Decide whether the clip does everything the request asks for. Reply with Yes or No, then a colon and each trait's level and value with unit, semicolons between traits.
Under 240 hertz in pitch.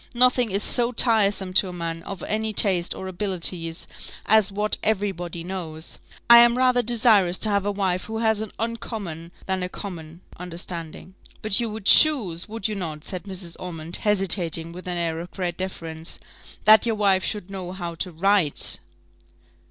Yes: high, 190 Hz